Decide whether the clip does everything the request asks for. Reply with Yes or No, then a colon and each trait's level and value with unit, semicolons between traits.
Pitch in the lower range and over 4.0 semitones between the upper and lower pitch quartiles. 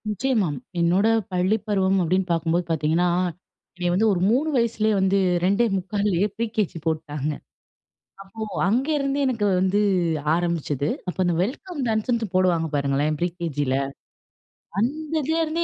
No: high, 190 Hz; average, 5.3 semitones